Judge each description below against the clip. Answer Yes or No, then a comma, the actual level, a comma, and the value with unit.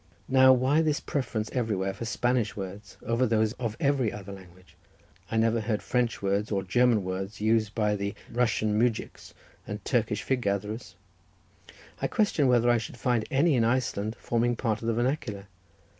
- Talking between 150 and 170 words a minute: Yes, average, 165 wpm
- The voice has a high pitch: No, low, 115 Hz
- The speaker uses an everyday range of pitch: Yes, average, 3.0 semitones